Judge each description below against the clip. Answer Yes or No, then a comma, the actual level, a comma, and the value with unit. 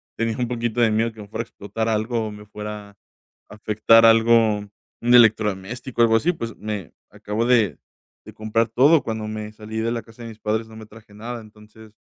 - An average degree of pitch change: No, narrow, 1.5 semitones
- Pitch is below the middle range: Yes, low, 110 Hz